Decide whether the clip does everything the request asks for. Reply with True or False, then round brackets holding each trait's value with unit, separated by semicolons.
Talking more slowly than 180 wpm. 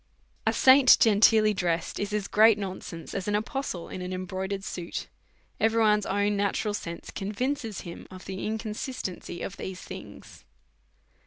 True (150 wpm)